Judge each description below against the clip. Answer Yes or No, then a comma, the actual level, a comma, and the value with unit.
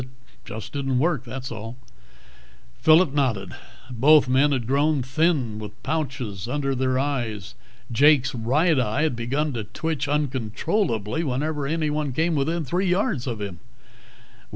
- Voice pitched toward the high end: No, low, 135 Hz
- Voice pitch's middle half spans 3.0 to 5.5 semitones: Yes, average, 4.3 semitones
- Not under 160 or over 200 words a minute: No, average, 140 wpm